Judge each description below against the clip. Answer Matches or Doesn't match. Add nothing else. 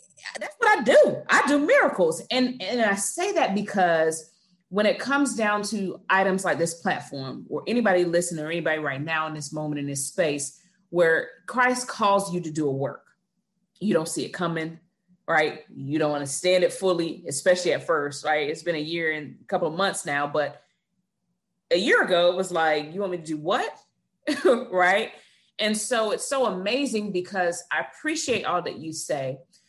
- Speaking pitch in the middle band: Matches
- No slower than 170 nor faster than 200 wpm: Matches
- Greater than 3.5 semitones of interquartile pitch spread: Matches